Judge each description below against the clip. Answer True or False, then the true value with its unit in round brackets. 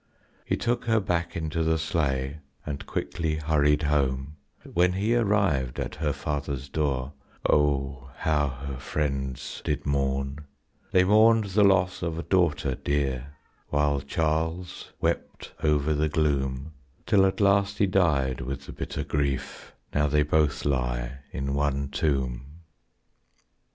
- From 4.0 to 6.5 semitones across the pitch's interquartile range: False (3.5 semitones)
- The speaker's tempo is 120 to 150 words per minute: True (135 wpm)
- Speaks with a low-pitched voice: True (75 Hz)